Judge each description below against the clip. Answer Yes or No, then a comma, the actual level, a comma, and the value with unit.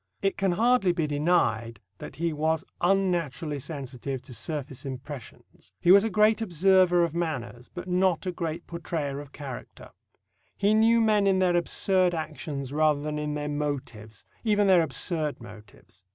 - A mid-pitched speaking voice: Yes, medium, 160 Hz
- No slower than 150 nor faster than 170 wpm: Yes, average, 160 wpm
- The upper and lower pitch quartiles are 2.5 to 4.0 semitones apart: No, average, 4.7 semitones